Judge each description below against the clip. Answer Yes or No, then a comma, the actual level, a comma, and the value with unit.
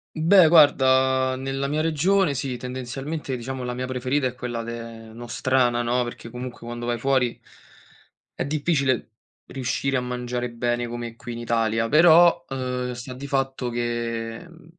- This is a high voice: No, low, 125 Hz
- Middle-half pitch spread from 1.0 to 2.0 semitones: No, narrow, 2.4 semitones